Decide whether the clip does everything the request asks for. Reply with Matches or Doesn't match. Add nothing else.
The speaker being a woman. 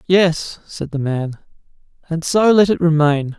Doesn't match